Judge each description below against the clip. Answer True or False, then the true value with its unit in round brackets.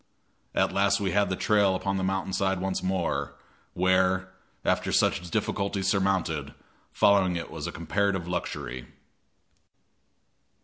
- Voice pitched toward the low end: True (95 Hz)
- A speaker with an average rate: False (130 wpm)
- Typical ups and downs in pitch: False (1.5 semitones)